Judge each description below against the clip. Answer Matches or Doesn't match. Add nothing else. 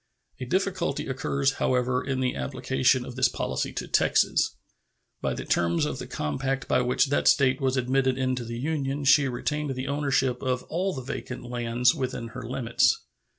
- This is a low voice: Matches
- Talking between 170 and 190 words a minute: Matches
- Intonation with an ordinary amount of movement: Doesn't match